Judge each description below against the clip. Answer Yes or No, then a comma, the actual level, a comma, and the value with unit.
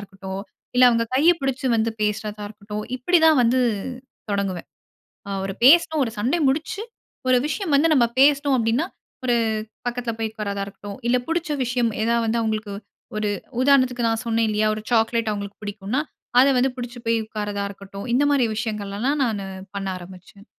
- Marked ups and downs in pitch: No, average, 4.1 semitones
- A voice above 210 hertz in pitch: Yes, high, 230 Hz